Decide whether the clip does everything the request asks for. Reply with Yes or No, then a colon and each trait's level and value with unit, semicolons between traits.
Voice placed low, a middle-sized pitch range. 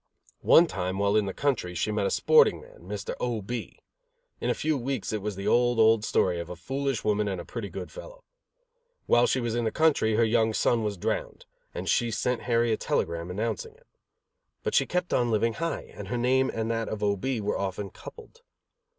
Yes: low, 115 Hz; average, 3.6 semitones